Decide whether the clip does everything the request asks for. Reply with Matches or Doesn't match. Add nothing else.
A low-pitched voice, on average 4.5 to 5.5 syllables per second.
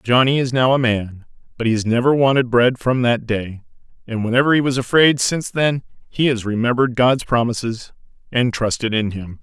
Matches